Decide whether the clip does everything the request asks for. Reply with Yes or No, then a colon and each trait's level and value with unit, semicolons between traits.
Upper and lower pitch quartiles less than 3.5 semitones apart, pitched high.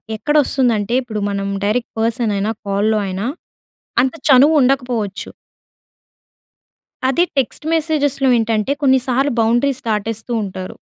No: average, 4.1 semitones; high, 235 Hz